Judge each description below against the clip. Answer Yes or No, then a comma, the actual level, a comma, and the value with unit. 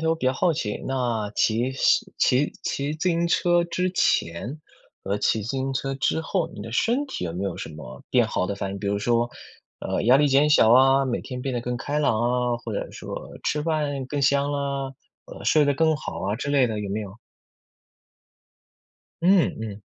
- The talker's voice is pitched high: No, low, 135 Hz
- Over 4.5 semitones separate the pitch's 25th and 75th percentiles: Yes, average, 4.9 semitones